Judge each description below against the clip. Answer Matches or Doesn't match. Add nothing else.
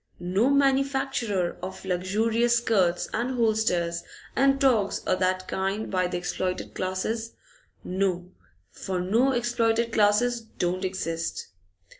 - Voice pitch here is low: Doesn't match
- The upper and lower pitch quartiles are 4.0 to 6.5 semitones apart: Matches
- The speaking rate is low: Matches